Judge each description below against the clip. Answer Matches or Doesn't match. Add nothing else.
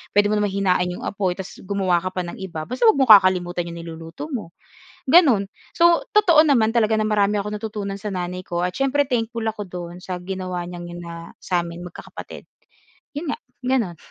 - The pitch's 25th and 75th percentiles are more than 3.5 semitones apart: Matches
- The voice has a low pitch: Doesn't match